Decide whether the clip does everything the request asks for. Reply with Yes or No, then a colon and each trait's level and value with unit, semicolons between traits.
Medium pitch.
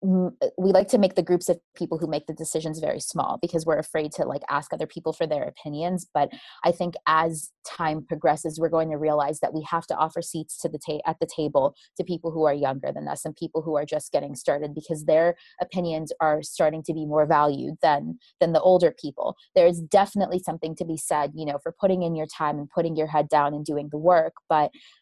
Yes: medium, 160 Hz